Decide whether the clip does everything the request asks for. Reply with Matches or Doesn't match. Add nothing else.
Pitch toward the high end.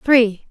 Matches